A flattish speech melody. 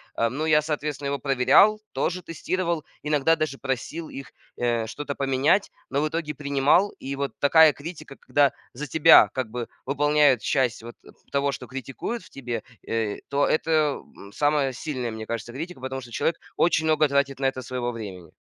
No: average, 3.3 semitones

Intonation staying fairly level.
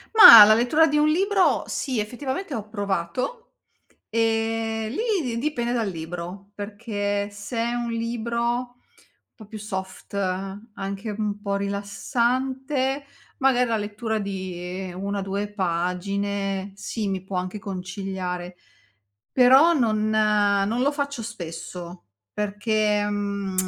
No: average, 3.3 semitones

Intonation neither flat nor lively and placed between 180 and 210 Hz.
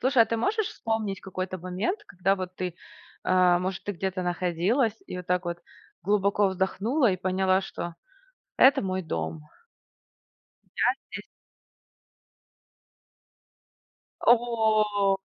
Yes: average, 3.2 semitones; high, 190 Hz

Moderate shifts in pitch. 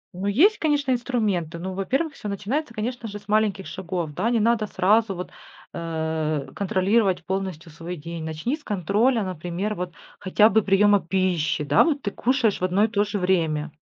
Yes: average, 4.2 semitones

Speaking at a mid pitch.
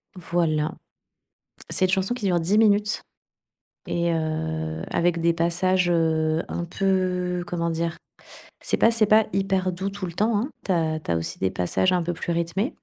Yes: medium, 175 Hz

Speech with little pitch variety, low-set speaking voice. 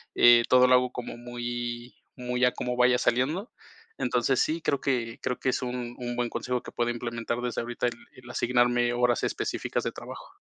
Yes: narrow, 0.8 semitones; low, 120 Hz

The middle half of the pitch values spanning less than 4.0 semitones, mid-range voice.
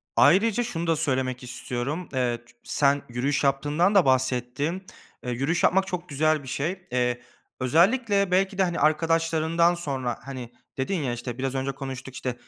No: average, 5.1 semitones; medium, 145 Hz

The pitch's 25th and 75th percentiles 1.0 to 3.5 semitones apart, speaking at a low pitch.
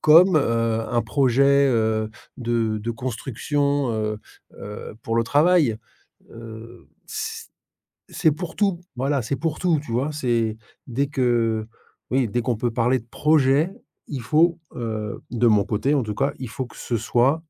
No: average, 4.0 semitones; low, 125 Hz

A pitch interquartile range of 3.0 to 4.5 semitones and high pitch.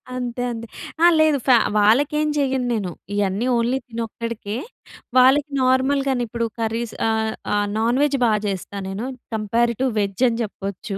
Yes: average, 3.4 semitones; high, 235 Hz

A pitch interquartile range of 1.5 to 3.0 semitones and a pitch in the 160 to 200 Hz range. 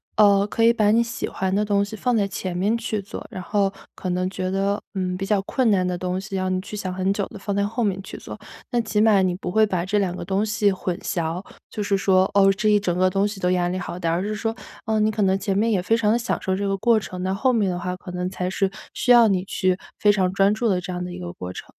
Yes: narrow, 2.4 semitones; high, 195 Hz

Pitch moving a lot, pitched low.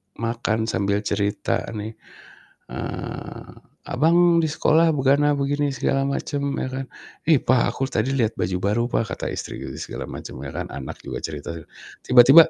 Yes: wide, 5.7 semitones; low, 130 Hz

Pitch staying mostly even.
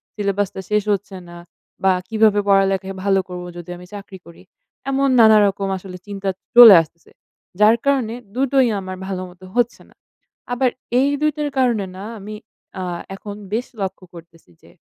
No: average, 3.2 semitones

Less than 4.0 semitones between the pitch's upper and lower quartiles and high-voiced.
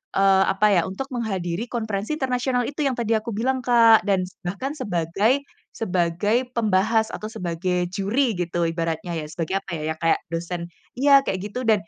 No: average, 5.2 semitones; high, 205 Hz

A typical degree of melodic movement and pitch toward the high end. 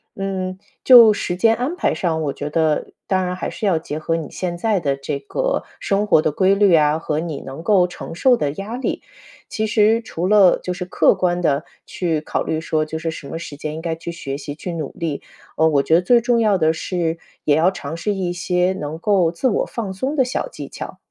No: average, 4.1 semitones; medium, 175 Hz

